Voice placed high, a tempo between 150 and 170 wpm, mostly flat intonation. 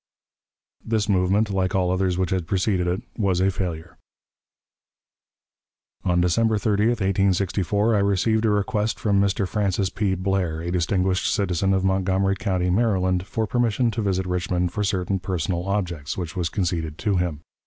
No: very low, 95 Hz; average, 155 wpm; narrow, 2.2 semitones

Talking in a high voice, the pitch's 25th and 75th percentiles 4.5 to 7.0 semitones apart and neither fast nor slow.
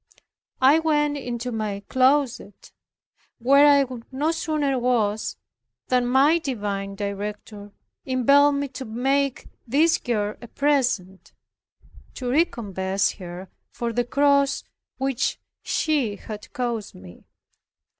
No: very high, 250 Hz; average, 5.1 semitones; slow, 110 wpm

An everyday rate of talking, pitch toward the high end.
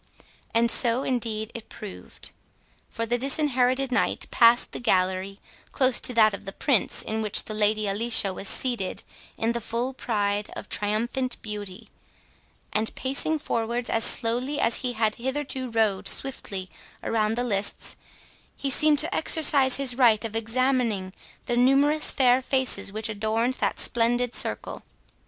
Yes: average, 150 wpm; high, 235 Hz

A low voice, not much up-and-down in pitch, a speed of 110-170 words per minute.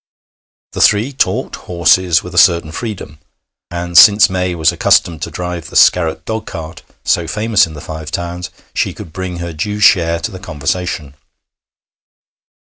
Yes: very low, 85 Hz; narrow, 2.3 semitones; average, 155 wpm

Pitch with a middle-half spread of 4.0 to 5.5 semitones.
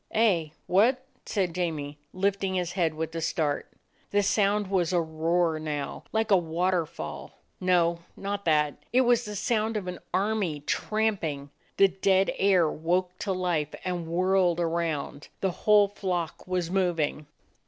No: average, 3.4 semitones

